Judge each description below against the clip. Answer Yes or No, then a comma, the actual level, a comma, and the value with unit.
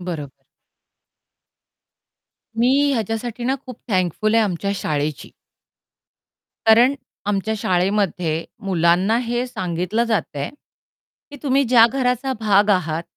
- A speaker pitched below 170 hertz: No, high, 205 Hz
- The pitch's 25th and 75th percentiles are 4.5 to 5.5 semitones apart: Yes, average, 5.0 semitones